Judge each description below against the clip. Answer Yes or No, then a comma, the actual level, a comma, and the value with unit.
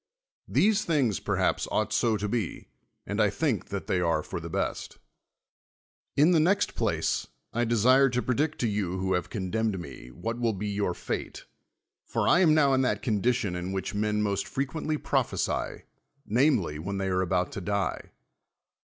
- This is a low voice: Yes, low, 105 Hz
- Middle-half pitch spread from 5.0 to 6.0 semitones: Yes, wide, 5.6 semitones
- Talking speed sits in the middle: Yes, average, 175 wpm